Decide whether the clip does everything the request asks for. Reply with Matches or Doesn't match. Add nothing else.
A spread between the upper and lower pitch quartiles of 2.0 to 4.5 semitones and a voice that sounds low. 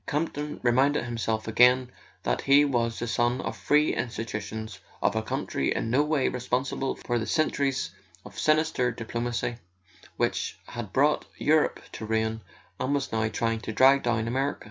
Matches